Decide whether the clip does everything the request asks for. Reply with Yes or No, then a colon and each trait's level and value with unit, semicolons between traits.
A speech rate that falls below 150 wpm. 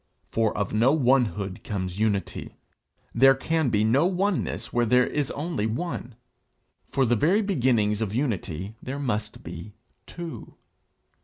Yes: average, 140 wpm